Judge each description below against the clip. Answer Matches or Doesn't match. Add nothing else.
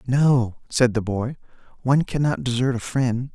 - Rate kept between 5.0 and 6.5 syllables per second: Doesn't match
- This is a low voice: Matches